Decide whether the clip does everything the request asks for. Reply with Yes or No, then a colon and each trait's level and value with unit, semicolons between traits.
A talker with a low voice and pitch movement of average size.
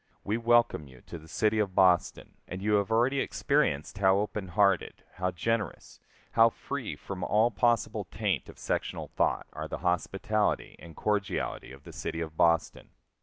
Yes: low, 100 Hz; average, 3.7 semitones